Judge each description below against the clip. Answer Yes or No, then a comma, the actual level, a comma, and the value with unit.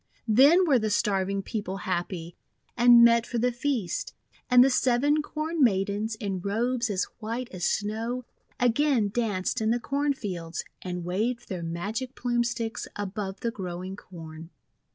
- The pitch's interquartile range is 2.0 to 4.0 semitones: No, average, 4.4 semitones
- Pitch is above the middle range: Yes, high, 220 Hz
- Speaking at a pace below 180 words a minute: Yes, average, 155 wpm